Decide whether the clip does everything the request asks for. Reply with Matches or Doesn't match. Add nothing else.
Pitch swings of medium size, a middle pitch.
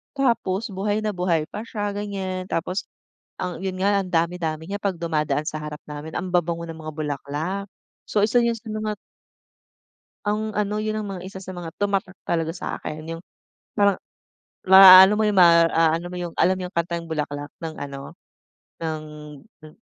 Matches